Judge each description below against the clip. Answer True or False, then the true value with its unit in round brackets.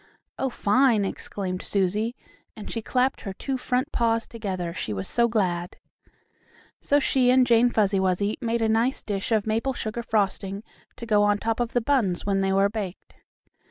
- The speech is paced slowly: False (180 wpm)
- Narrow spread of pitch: False (3.4 semitones)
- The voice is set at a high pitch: True (220 Hz)